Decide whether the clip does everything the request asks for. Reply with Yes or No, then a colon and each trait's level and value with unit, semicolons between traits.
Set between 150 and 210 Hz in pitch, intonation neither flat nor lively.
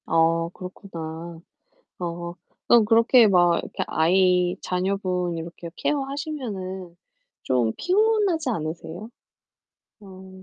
Yes: medium, 185 Hz; average, 4.9 semitones